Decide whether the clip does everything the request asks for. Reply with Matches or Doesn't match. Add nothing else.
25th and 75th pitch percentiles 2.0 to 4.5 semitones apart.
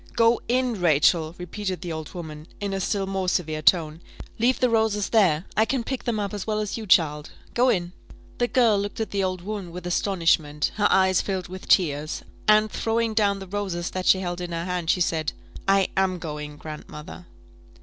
Matches